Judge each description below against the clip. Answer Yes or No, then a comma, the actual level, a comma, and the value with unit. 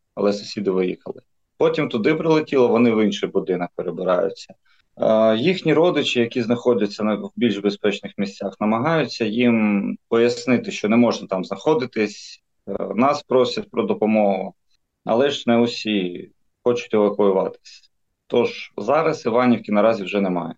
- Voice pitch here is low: Yes, low, 110 Hz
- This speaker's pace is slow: No, average, 125 wpm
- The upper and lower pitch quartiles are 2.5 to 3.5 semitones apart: Yes, average, 3.1 semitones